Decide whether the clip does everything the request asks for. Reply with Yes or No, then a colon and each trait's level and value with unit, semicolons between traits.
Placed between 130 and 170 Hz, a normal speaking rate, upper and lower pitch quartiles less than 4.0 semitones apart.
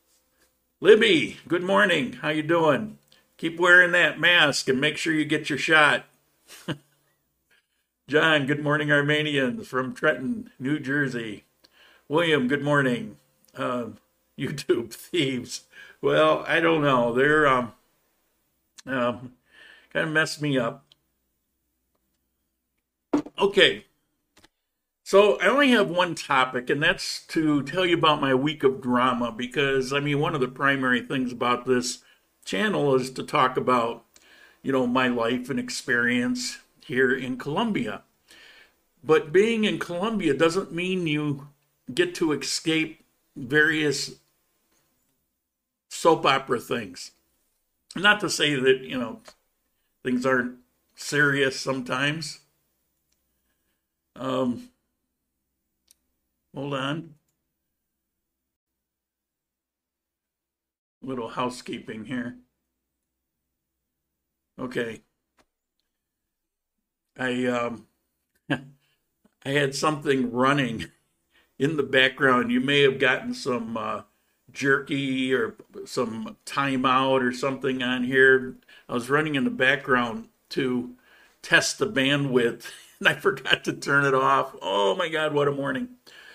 No: low, 135 Hz; slow, 115 wpm; average, 3.6 semitones